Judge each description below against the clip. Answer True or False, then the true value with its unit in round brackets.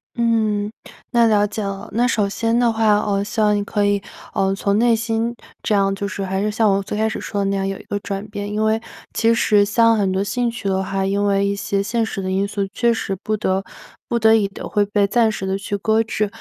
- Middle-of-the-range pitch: False (205 Hz)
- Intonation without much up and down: True (2.0 semitones)